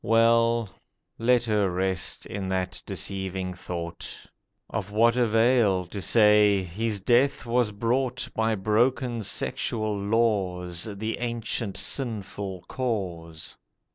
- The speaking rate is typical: No, slow, 110 wpm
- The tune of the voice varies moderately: Yes, average, 3.6 semitones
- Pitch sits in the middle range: No, low, 105 Hz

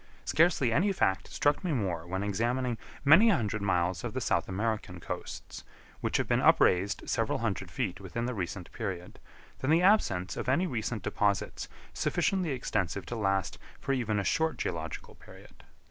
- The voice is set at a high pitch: No, low, 110 Hz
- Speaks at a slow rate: No, average, 165 wpm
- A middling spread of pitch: No, wide, 5.7 semitones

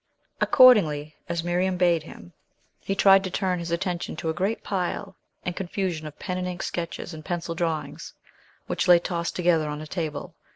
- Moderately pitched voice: Yes, medium, 175 Hz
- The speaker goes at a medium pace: Yes, average, 180 wpm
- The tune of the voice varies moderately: No, narrow, 2.3 semitones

